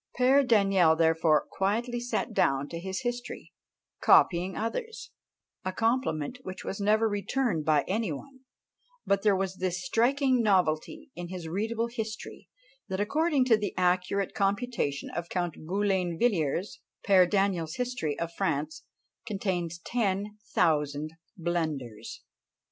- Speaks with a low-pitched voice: No, high, 195 Hz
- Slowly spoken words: Yes, slow, 125 wpm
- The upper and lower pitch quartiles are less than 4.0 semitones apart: No, average, 5.3 semitones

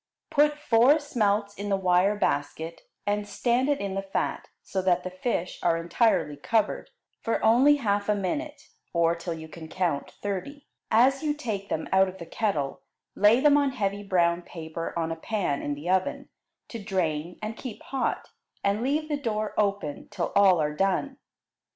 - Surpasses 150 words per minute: Yes, average, 180 wpm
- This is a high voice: Yes, high, 200 Hz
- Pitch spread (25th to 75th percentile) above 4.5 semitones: Yes, wide, 5.4 semitones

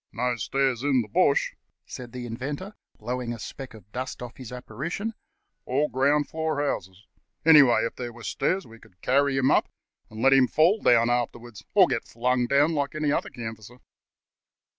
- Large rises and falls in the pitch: No, average, 3.3 semitones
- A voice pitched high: No, low, 125 Hz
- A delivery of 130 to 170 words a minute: No, average, 180 wpm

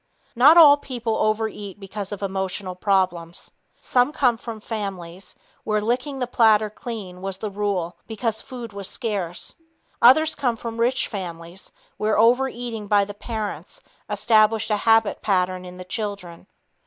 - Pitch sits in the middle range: No, high, 210 Hz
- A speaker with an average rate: Yes, average, 145 wpm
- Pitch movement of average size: Yes, average, 3.4 semitones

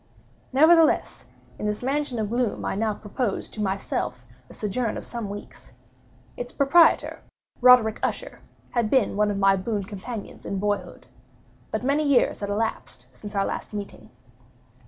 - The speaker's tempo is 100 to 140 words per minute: No, average, 155 wpm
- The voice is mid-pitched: No, high, 220 Hz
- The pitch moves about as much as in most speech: Yes, average, 3.7 semitones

